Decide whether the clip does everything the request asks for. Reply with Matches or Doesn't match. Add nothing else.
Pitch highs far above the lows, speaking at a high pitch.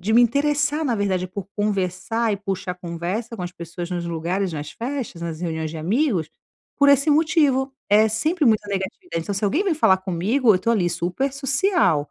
Matches